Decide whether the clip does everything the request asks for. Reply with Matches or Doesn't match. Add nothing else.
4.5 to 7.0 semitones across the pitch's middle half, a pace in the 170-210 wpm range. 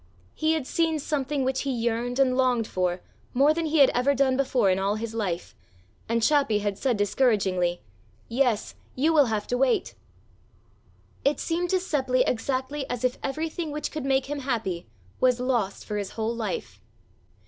Doesn't match